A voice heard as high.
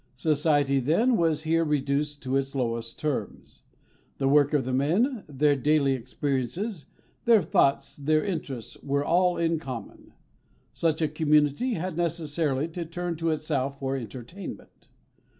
No: medium, 150 Hz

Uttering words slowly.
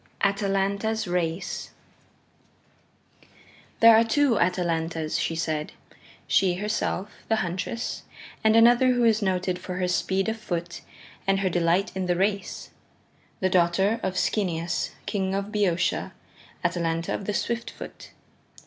Yes: slow, 130 wpm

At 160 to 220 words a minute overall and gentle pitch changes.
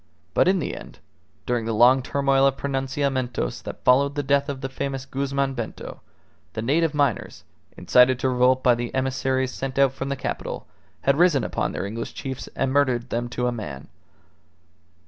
Yes: average, 180 wpm; narrow, 2.0 semitones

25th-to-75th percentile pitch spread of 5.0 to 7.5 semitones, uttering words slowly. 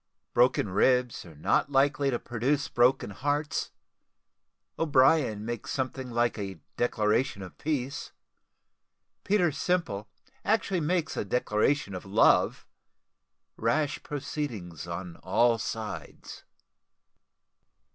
Yes: wide, 5.5 semitones; slow, 95 wpm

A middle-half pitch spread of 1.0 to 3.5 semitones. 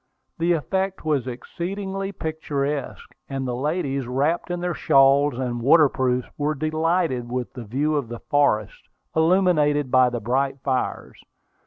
No: average, 4.3 semitones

